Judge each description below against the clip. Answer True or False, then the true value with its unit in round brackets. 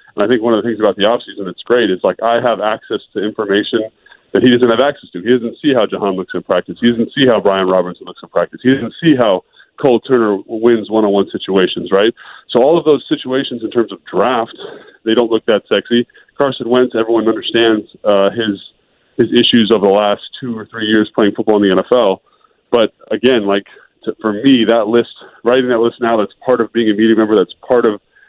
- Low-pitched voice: True (115 Hz)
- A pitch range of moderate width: False (2.3 semitones)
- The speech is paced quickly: True (225 wpm)